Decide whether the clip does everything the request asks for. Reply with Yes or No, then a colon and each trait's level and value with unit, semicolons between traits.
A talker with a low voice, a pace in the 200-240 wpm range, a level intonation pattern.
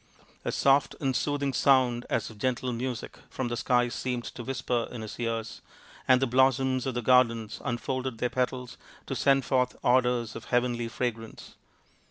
No: low, 125 Hz; average, 170 wpm; narrow, 1.7 semitones